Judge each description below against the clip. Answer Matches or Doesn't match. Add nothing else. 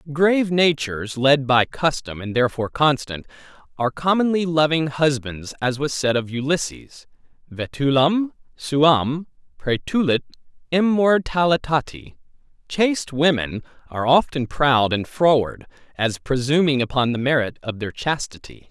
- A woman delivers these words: Doesn't match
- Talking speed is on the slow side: Matches